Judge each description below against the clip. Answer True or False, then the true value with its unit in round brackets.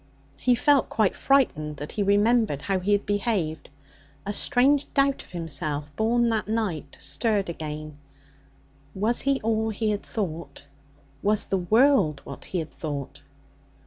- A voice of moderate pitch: False (205 Hz)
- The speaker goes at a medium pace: True (145 wpm)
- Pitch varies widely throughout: True (6.6 semitones)